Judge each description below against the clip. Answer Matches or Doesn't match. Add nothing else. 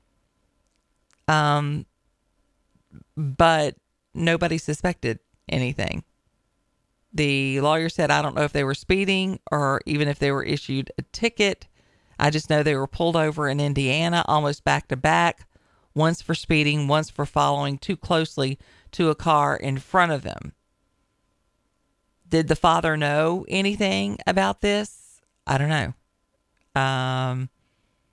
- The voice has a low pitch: Doesn't match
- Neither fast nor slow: Doesn't match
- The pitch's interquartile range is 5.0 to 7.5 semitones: Doesn't match